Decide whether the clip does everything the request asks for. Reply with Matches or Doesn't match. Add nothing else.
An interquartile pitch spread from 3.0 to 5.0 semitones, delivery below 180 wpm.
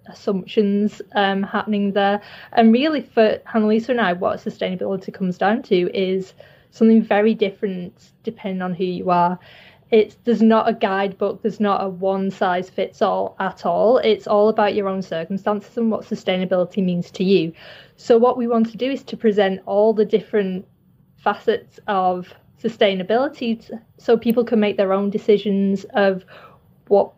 Doesn't match